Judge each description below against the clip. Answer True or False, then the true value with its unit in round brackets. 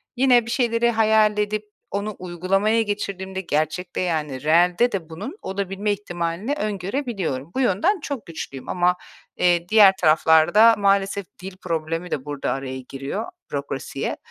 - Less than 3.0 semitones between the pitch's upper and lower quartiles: False (4.4 semitones)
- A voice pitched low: False (190 Hz)